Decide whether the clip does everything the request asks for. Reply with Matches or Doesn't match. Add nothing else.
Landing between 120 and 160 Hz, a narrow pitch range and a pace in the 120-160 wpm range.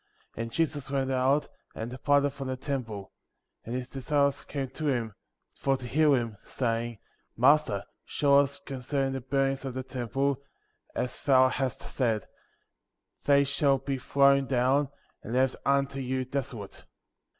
Matches